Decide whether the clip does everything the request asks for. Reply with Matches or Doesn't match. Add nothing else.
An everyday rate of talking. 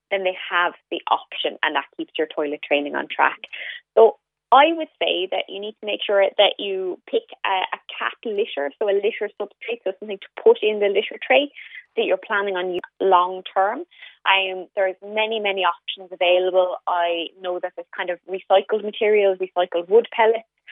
Matches